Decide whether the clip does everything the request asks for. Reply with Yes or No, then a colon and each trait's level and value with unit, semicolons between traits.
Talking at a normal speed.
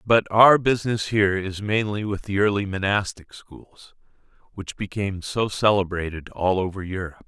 Yes: average, 150 wpm